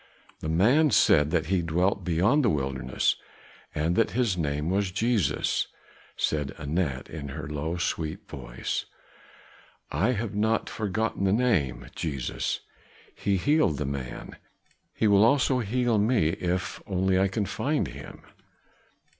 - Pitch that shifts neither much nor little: No, wide, 6.1 semitones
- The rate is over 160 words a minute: No, average, 140 wpm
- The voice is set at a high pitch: No, very low, 95 Hz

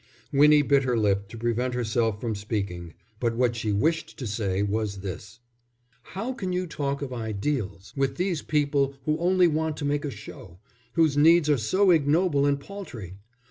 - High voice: No, low, 135 Hz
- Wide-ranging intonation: Yes, wide, 5.9 semitones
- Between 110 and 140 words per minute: No, average, 180 wpm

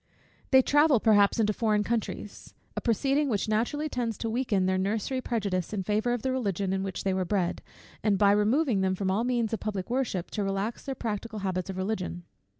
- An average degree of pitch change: Yes, average, 3.7 semitones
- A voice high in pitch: Yes, high, 210 Hz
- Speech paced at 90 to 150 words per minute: No, fast, 205 wpm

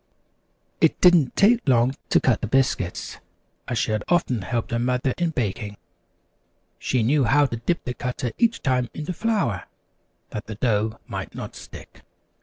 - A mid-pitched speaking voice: No, low, 125 Hz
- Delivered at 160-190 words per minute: Yes, average, 165 wpm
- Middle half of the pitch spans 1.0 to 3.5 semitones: No, average, 4.7 semitones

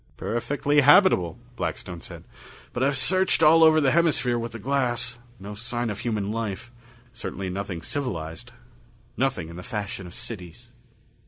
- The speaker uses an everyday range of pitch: No, wide, 6.0 semitones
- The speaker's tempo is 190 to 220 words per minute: No, average, 150 wpm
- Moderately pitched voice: No, low, 120 Hz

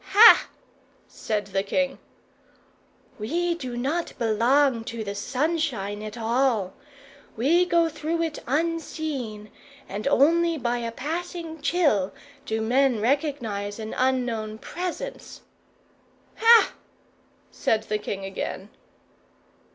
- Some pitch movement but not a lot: No, wide, 6.9 semitones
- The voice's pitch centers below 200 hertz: No, very high, 255 Hz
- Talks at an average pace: No, slow, 105 wpm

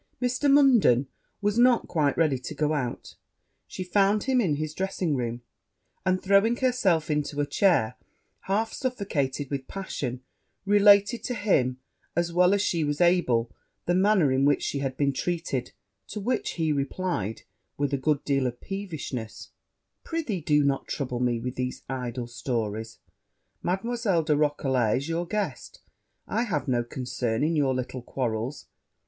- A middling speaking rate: Yes, average, 155 wpm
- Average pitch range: No, wide, 7.1 semitones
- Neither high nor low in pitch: Yes, medium, 150 Hz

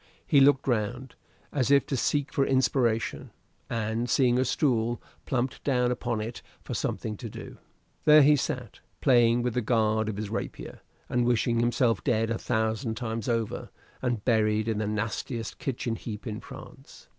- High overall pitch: No, low, 120 Hz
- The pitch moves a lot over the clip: No, narrow, 2.5 semitones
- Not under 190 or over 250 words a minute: No, average, 170 wpm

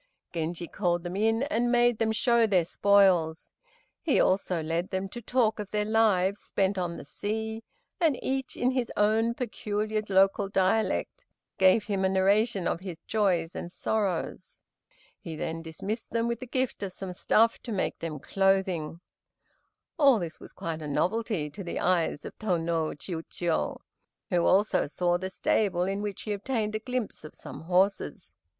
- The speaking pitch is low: No, high, 195 Hz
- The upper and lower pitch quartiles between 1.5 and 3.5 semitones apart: No, average, 4.1 semitones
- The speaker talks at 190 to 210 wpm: No, average, 170 wpm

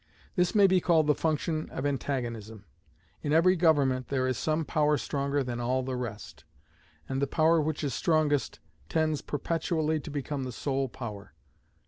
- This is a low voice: No, medium, 145 Hz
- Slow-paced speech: No, average, 165 wpm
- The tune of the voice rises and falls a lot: No, average, 3.4 semitones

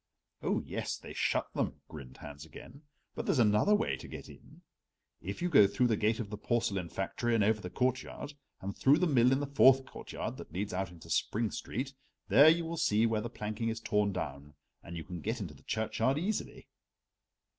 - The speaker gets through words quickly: Yes, fast, 210 wpm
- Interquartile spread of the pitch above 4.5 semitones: Yes, wide, 5.4 semitones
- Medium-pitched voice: No, low, 110 Hz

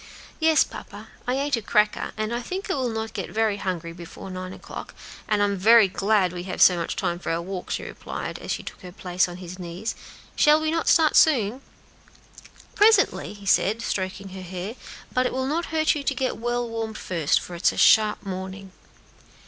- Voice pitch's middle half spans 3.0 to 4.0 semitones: No, wide, 5.5 semitones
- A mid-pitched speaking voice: No, high, 210 Hz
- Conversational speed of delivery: No, fast, 210 wpm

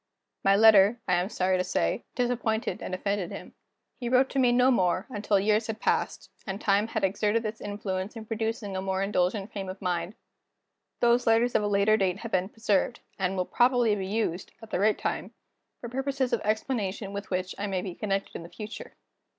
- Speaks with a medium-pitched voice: No, high, 205 Hz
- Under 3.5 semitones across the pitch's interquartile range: Yes, average, 3.0 semitones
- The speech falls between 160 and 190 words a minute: No, fast, 205 wpm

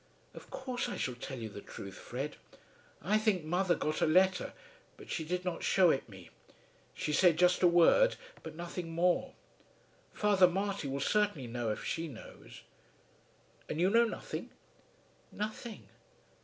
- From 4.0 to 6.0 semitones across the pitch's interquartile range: Yes, average, 5.0 semitones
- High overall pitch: No, medium, 175 Hz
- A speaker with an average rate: Yes, average, 155 wpm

